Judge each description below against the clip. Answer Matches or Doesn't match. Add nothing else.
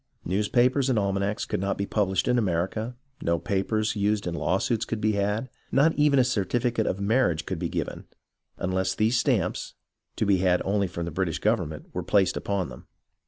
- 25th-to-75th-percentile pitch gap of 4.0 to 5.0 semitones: Doesn't match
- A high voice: Doesn't match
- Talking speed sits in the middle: Matches